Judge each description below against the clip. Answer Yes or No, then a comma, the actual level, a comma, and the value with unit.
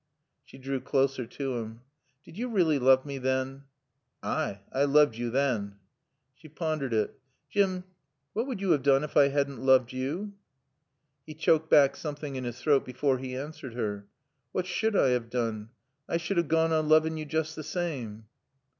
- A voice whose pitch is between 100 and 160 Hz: Yes, medium, 140 Hz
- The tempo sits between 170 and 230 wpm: Yes, average, 180 wpm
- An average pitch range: Yes, average, 3.7 semitones